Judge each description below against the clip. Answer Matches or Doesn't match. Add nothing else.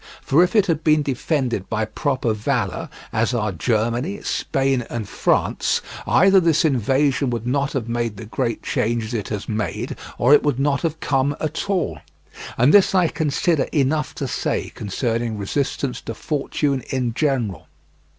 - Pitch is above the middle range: Doesn't match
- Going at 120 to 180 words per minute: Matches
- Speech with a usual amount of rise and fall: Matches